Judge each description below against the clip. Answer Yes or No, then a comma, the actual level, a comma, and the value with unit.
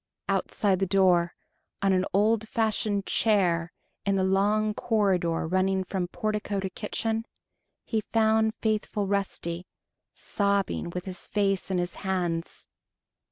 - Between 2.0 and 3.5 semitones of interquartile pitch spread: Yes, narrow, 2.5 semitones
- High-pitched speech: Yes, high, 195 Hz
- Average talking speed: No, slow, 125 wpm